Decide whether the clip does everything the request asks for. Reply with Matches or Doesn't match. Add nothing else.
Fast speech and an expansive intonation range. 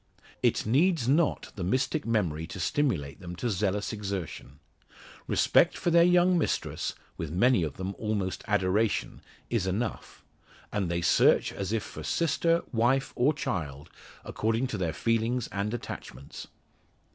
Doesn't match